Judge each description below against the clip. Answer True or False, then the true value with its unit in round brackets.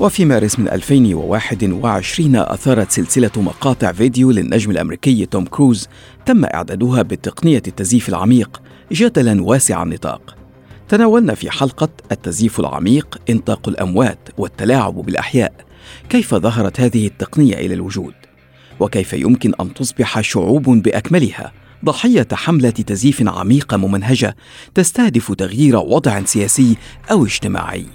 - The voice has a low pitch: True (115 Hz)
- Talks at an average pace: True (110 wpm)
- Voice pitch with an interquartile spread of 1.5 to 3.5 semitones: False (5.2 semitones)